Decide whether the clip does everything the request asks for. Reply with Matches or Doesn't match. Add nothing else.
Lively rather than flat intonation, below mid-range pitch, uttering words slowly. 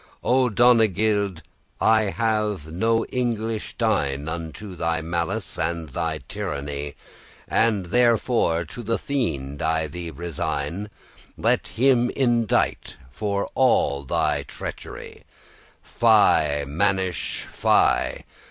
Matches